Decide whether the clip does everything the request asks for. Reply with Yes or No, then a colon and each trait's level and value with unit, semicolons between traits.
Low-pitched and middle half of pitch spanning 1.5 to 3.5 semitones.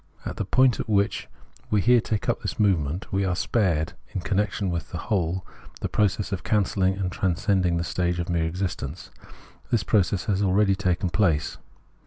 Yes: very low, 95 Hz; average, 2.9 semitones